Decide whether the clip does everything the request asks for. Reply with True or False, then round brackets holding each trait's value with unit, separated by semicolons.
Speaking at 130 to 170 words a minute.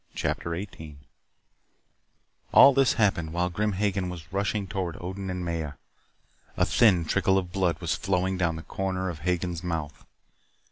True (150 wpm)